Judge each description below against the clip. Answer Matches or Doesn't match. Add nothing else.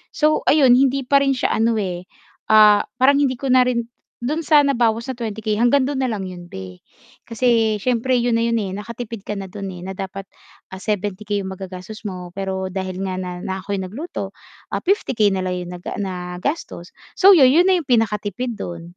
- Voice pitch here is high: Matches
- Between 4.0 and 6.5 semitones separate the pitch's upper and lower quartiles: Matches